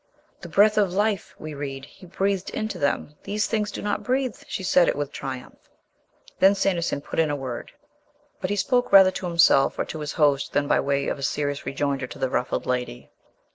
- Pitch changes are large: Yes, wide, 5.9 semitones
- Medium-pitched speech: Yes, medium, 165 Hz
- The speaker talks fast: Yes, fast, 210 wpm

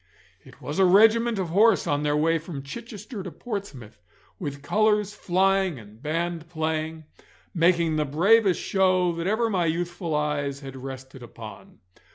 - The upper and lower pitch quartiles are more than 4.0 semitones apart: Yes, average, 4.8 semitones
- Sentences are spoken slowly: No, average, 155 wpm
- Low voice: No, medium, 170 Hz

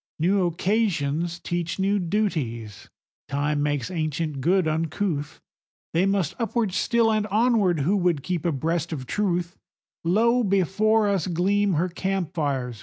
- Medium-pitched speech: Yes, medium, 175 Hz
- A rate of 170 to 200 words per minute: No, slow, 135 wpm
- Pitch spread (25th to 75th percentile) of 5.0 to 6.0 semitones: No, average, 4.6 semitones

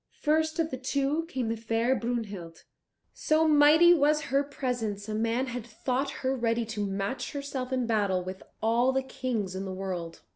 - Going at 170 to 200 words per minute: Yes, average, 180 wpm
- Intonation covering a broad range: No, average, 4.5 semitones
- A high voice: Yes, high, 245 Hz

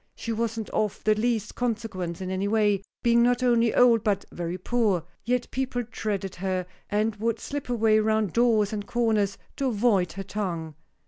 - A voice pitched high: Yes, high, 215 Hz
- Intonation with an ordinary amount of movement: Yes, average, 3.2 semitones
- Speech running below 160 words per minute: No, average, 175 wpm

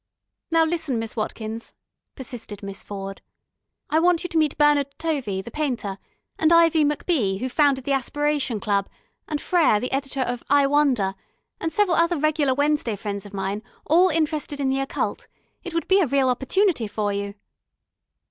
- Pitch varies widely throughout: Yes, wide, 6.3 semitones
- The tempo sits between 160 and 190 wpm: Yes, average, 170 wpm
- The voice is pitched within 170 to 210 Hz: No, very high, 275 Hz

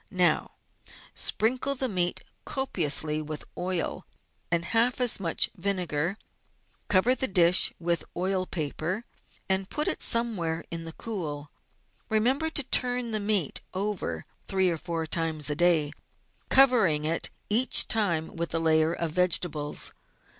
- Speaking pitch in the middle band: Yes, medium, 180 Hz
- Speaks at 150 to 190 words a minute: No, slow, 135 wpm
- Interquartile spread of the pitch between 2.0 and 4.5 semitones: No, average, 5.2 semitones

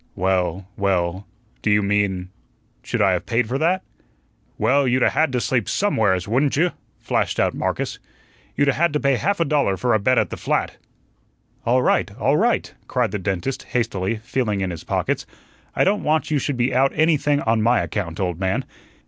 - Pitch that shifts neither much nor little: No, wide, 6.3 semitones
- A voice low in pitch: Yes, low, 115 Hz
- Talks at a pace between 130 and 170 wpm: No, average, 195 wpm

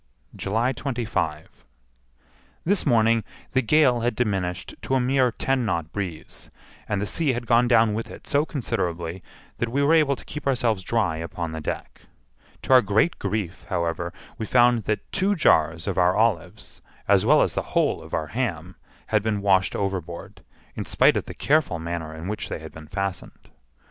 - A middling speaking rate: Yes, average, 180 wpm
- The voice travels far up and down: Yes, wide, 6.0 semitones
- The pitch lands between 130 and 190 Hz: No, low, 105 Hz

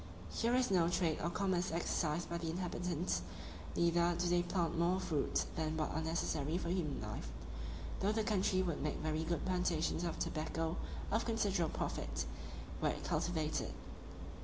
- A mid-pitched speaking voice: Yes, medium, 170 Hz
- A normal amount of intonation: No, narrow, 2.3 semitones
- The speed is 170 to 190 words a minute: No, average, 160 wpm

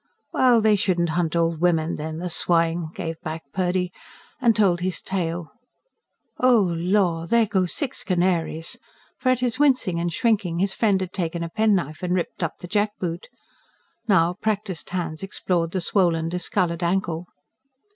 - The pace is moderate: Yes, average, 155 wpm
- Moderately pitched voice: Yes, medium, 180 Hz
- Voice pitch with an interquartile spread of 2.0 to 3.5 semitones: Yes, average, 3.1 semitones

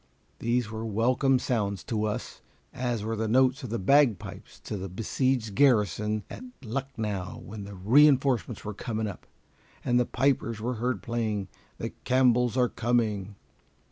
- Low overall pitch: Yes, low, 115 Hz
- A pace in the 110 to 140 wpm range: No, average, 155 wpm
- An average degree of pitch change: Yes, average, 3.0 semitones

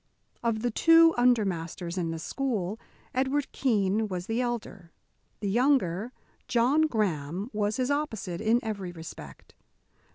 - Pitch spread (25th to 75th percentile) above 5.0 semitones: Yes, wide, 5.4 semitones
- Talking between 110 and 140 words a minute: Yes, slow, 135 wpm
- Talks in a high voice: Yes, high, 220 Hz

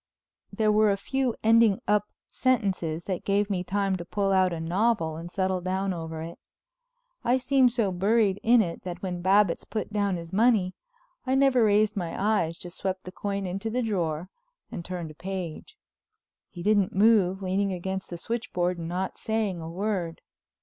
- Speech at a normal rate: Yes, average, 180 wpm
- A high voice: Yes, high, 195 Hz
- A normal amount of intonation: Yes, average, 3.3 semitones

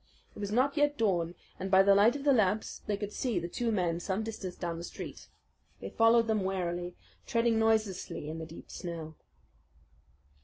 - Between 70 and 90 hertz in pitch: No, high, 200 Hz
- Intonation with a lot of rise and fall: No, average, 4.3 semitones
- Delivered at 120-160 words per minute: No, average, 190 wpm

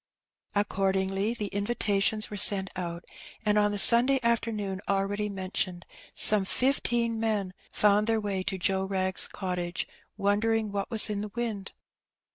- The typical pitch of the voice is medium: No, high, 205 Hz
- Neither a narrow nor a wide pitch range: No, narrow, 2.3 semitones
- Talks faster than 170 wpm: No, average, 145 wpm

